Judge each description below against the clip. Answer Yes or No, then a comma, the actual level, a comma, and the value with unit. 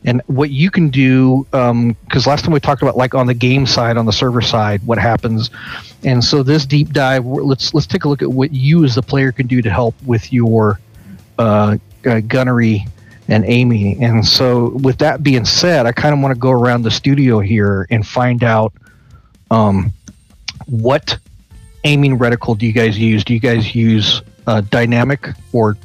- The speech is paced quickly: No, average, 195 wpm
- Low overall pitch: Yes, low, 120 Hz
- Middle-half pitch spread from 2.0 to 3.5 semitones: Yes, average, 3.2 semitones